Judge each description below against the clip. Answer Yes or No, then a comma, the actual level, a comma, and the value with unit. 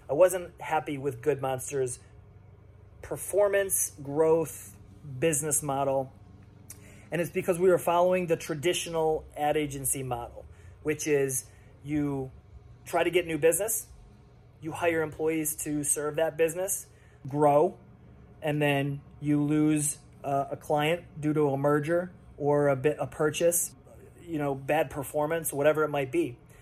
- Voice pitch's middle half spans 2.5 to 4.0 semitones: Yes, average, 3.3 semitones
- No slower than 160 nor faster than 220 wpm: No, average, 140 wpm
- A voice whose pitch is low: No, medium, 150 Hz